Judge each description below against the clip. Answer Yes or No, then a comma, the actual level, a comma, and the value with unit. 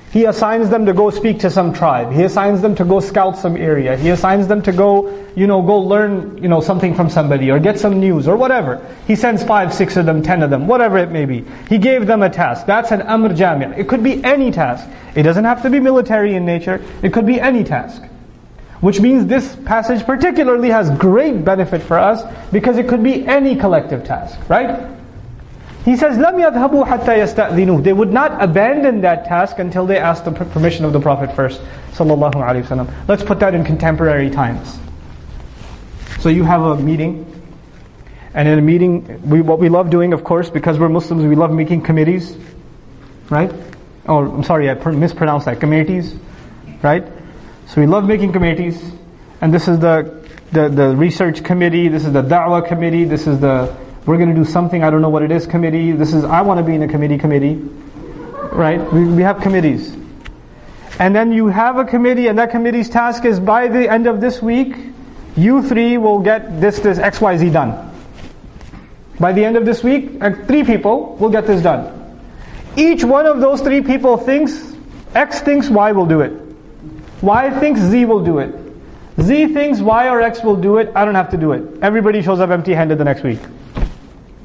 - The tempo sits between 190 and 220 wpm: Yes, average, 200 wpm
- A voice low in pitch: No, medium, 185 Hz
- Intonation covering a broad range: Yes, wide, 5.8 semitones